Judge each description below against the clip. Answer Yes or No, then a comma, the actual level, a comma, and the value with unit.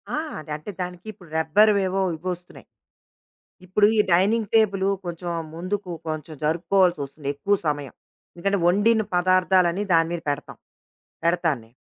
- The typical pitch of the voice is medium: Yes, medium, 180 Hz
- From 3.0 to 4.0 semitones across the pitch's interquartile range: Yes, average, 3.5 semitones